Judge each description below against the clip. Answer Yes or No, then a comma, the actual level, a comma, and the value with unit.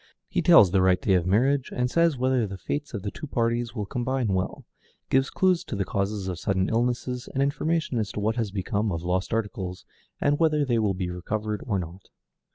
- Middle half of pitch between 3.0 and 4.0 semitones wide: No, average, 5.2 semitones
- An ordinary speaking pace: No, fast, 215 wpm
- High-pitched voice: No, low, 110 Hz